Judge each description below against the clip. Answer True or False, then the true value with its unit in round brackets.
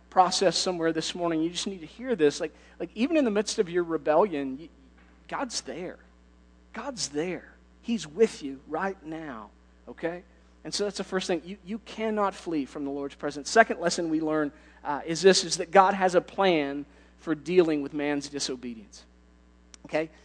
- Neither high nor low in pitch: True (165 Hz)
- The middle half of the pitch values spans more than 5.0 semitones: True (5.4 semitones)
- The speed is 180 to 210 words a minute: True (185 wpm)